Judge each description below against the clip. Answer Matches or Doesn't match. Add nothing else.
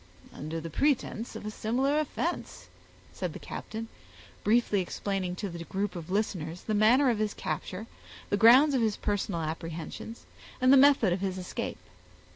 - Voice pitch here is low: Doesn't match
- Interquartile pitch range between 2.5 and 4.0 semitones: Doesn't match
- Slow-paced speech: Doesn't match